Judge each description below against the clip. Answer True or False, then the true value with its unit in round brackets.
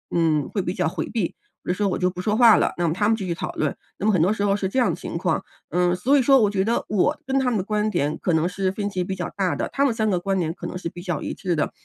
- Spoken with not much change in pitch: False (3.5 semitones)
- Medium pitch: False (195 Hz)